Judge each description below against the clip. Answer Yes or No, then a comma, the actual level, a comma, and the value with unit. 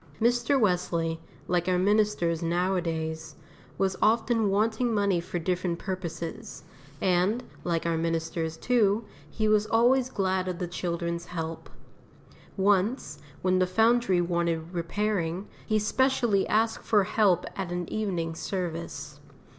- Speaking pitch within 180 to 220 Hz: Yes, medium, 185 Hz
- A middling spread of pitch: Yes, average, 4.0 semitones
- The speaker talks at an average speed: No, slow, 125 wpm